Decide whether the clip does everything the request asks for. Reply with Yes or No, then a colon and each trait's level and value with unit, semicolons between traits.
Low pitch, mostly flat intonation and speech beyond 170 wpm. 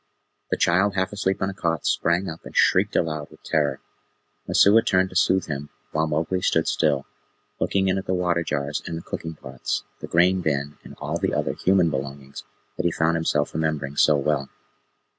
No: very low, 80 Hz; average, 4.0 semitones; average, 195 wpm